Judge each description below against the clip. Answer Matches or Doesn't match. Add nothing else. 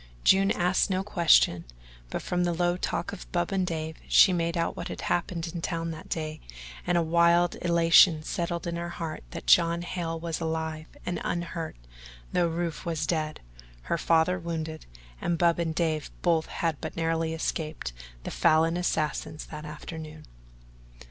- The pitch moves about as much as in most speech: Doesn't match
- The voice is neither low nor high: Matches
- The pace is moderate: Matches